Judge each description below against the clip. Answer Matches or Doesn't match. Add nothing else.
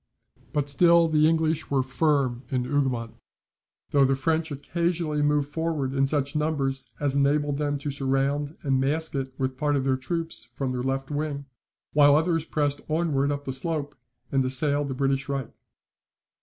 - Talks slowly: Doesn't match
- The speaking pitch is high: Doesn't match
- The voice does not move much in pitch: Matches